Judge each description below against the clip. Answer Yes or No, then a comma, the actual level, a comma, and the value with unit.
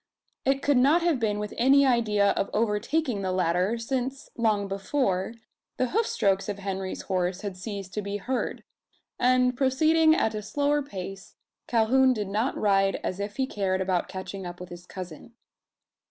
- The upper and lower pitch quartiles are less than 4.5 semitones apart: No, average, 5.2 semitones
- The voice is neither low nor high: No, high, 210 Hz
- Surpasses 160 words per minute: Yes, average, 170 wpm